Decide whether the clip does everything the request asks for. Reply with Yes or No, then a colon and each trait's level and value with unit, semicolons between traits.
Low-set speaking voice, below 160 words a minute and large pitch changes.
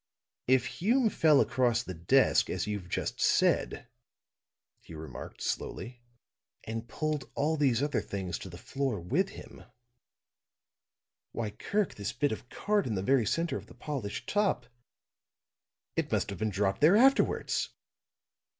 Yes: low, 125 Hz; average, 140 wpm; wide, 7.1 semitones